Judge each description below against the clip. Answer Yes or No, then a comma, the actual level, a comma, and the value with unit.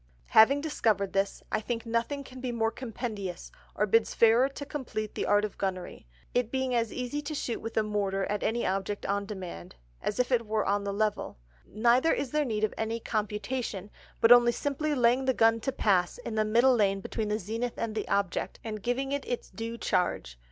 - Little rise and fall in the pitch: No, average, 3.2 semitones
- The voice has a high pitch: Yes, high, 225 Hz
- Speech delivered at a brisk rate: Yes, fast, 210 wpm